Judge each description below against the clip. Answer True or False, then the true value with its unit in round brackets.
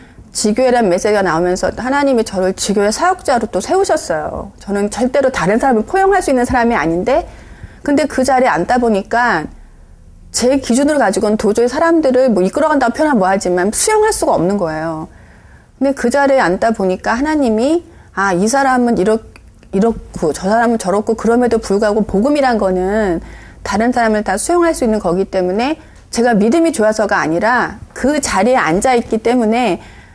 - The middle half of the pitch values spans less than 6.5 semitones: True (5.4 semitones)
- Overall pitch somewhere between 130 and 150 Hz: False (230 Hz)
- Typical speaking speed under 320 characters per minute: False (380 characters per minute)